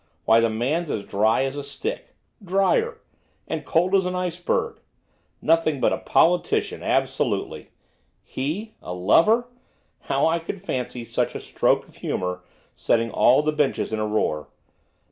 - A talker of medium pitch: Yes, medium, 150 Hz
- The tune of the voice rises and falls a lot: Yes, wide, 7.7 semitones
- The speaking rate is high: No, average, 150 wpm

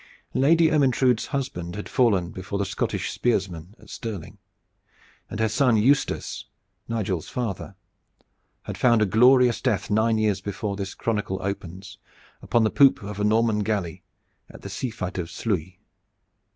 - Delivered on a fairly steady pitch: No, average, 3.7 semitones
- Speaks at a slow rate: No, average, 150 wpm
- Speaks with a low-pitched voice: Yes, low, 105 Hz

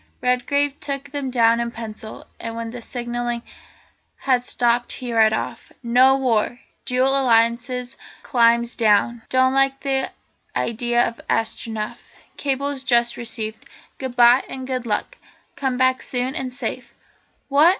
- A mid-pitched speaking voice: No, high, 245 Hz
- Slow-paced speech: Yes, slow, 130 wpm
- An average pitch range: No, narrow, 2.1 semitones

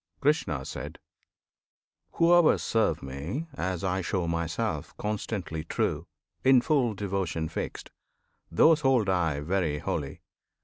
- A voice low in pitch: Yes, very low, 95 Hz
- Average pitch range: No, wide, 6.3 semitones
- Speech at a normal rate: No, slow, 105 wpm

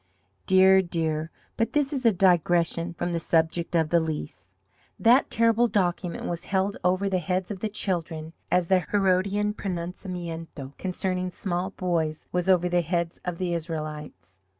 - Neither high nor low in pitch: Yes, medium, 180 Hz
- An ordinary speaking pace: Yes, average, 155 wpm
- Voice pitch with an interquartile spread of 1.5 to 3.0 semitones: Yes, narrow, 2.4 semitones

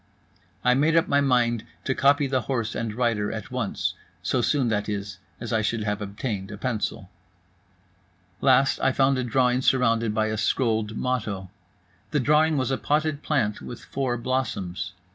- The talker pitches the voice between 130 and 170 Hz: No, low, 120 Hz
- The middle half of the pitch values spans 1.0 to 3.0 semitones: No, average, 3.7 semitones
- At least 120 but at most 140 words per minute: No, average, 170 wpm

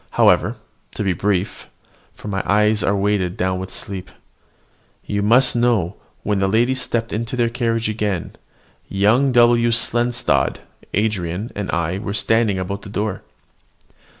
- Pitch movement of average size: Yes, average, 3.2 semitones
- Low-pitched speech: Yes, low, 105 Hz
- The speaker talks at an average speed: Yes, average, 150 wpm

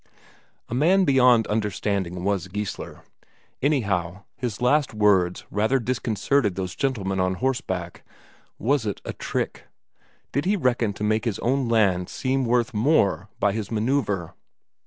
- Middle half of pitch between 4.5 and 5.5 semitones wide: Yes, average, 4.9 semitones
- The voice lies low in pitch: Yes, low, 110 Hz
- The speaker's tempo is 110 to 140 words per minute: Yes, slow, 135 wpm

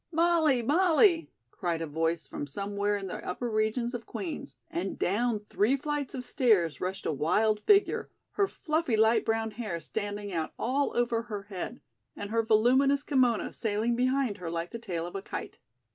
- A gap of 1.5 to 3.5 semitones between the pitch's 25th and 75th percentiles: No, average, 4.7 semitones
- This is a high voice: Yes, high, 220 Hz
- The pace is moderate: Yes, average, 175 wpm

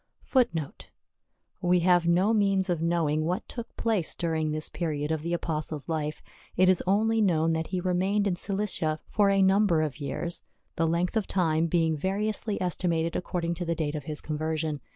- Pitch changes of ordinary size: Yes, average, 3.2 semitones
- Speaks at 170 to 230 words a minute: Yes, average, 180 wpm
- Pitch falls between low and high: Yes, medium, 170 Hz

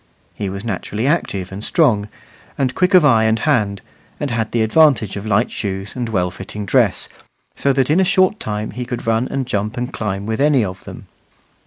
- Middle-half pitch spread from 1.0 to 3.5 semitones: No, average, 4.9 semitones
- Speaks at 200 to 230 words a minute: Yes, fast, 205 wpm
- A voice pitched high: No, low, 110 Hz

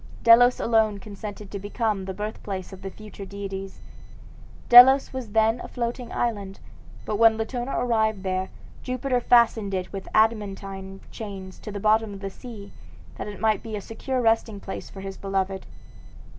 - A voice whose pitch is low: No, high, 210 Hz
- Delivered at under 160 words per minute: No, average, 165 wpm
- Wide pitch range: No, average, 2.7 semitones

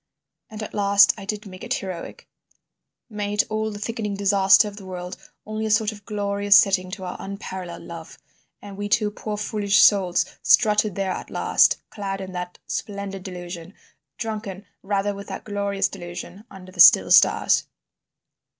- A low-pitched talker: No, high, 200 Hz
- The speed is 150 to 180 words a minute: Yes, average, 165 wpm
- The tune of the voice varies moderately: No, narrow, 1.7 semitones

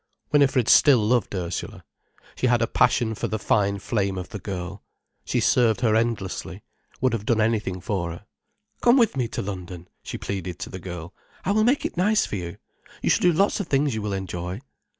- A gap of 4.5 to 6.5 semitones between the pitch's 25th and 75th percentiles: Yes, average, 5.2 semitones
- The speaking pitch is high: No, low, 110 Hz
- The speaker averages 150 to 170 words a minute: No, average, 200 wpm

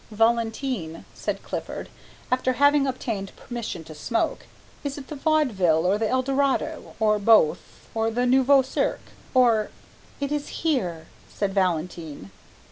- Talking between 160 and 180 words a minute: No, slow, 135 wpm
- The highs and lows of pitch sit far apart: Yes, wide, 5.7 semitones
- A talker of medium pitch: No, high, 230 Hz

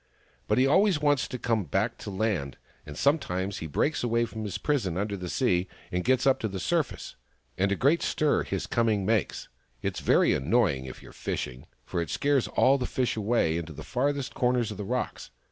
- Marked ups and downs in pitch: Yes, wide, 6.1 semitones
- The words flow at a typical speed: No, fast, 215 wpm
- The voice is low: Yes, low, 110 Hz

